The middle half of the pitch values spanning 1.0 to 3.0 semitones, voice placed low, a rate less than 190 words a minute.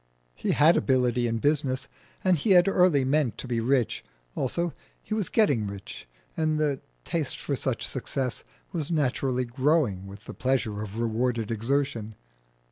No: average, 4.8 semitones; low, 130 Hz; average, 155 wpm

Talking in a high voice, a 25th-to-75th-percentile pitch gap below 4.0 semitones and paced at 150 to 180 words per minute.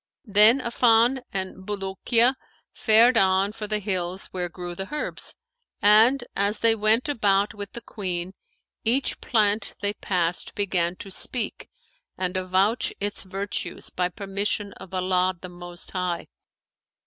No: high, 200 Hz; average, 2.9 semitones; slow, 135 wpm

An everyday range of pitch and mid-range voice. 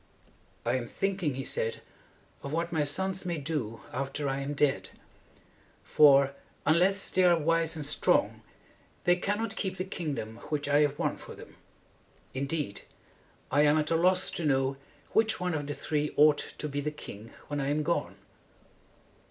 Yes: average, 3.8 semitones; medium, 150 Hz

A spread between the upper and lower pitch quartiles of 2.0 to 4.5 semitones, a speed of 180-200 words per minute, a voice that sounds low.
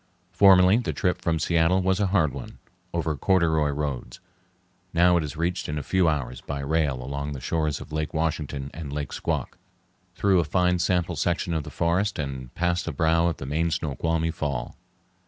Yes: average, 3.1 semitones; average, 190 wpm; very low, 80 Hz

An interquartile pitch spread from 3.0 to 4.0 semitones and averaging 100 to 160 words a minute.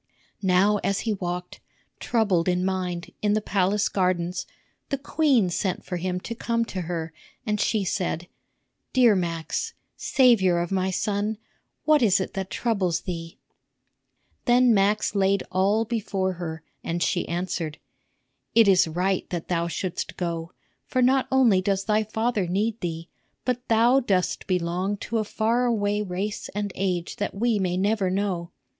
Yes: average, 3.4 semitones; average, 155 wpm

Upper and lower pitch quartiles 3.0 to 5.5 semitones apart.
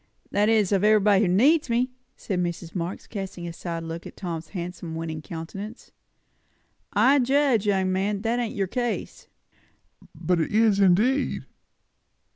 Yes: average, 4.5 semitones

